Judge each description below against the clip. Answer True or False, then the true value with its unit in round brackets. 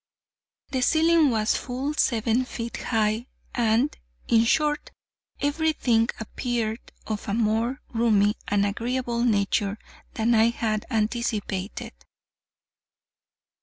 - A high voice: True (230 Hz)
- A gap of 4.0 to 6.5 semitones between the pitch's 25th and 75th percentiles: False (2.6 semitones)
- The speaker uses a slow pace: True (105 wpm)